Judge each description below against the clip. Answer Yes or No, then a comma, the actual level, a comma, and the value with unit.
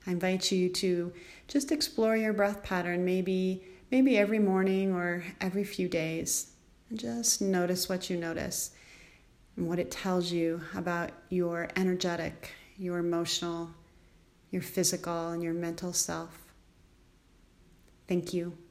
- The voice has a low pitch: No, medium, 180 Hz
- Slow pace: Yes, slow, 130 wpm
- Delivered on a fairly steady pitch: Yes, narrow, 1.9 semitones